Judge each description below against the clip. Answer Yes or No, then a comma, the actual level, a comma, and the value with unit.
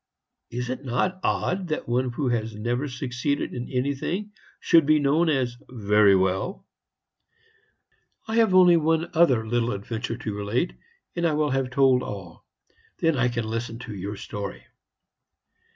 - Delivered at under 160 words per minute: Yes, average, 150 wpm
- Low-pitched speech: Yes, low, 125 Hz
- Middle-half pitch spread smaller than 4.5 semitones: No, average, 5.3 semitones